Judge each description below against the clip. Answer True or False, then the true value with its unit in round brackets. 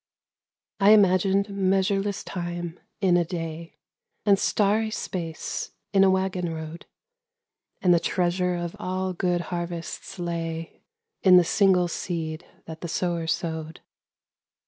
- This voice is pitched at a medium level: True (180 Hz)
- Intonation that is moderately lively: False (2.2 semitones)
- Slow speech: True (125 wpm)